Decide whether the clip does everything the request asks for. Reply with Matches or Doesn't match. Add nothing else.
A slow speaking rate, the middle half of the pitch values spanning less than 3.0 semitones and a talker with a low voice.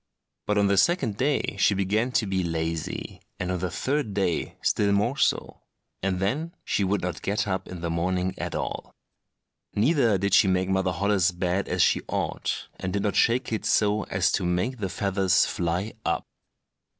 Doesn't match